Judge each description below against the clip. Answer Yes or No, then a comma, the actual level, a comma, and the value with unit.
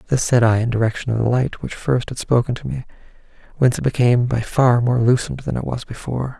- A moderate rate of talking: No, fast, 235 wpm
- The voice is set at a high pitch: No, low, 120 Hz